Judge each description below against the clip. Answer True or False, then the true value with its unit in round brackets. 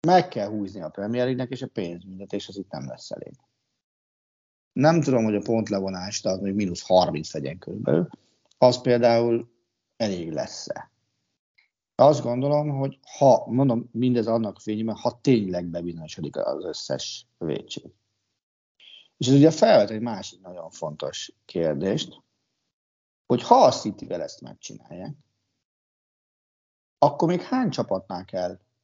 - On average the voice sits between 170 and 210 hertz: False (115 Hz)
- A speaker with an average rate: True (135 wpm)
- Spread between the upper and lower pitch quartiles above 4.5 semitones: True (5.3 semitones)